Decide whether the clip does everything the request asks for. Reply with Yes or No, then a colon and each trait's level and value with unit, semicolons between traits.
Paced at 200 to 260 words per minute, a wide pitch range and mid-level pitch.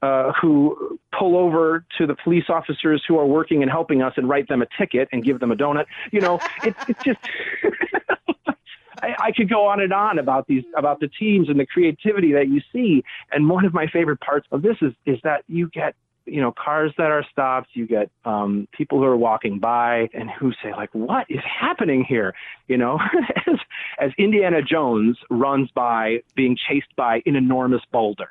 Yes: fast, 205 wpm; wide, 6.1 semitones; medium, 150 Hz